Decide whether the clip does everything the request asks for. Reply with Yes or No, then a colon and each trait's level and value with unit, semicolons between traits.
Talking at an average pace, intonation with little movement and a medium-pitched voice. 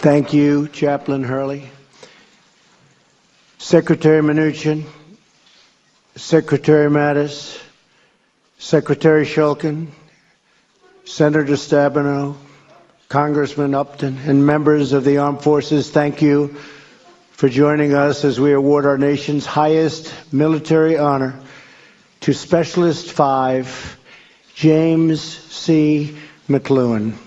No: slow, 85 wpm; narrow, 1.6 semitones; medium, 145 Hz